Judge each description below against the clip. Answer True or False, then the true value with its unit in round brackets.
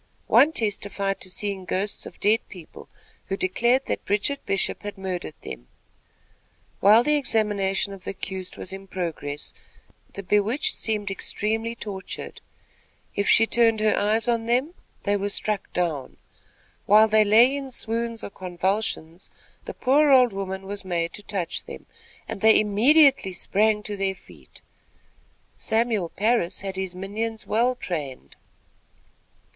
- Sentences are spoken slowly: False (145 wpm)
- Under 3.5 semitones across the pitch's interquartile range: True (3.0 semitones)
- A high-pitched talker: True (205 Hz)